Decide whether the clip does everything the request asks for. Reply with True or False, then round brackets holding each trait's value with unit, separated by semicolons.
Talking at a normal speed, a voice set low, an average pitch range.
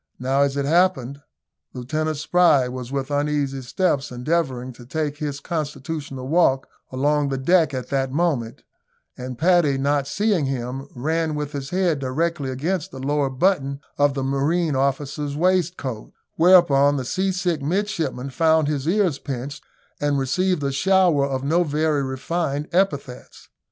False (145 wpm; 145 Hz; 3.7 semitones)